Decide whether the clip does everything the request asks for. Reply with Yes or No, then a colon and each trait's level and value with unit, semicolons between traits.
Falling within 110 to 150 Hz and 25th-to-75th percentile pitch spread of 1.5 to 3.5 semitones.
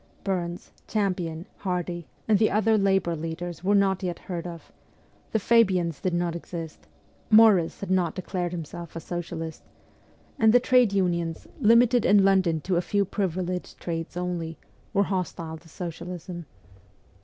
No: medium, 180 Hz; average, 2.7 semitones